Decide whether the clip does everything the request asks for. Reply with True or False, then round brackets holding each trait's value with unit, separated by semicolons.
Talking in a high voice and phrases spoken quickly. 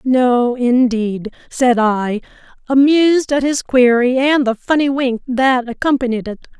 False (250 Hz; 135 wpm)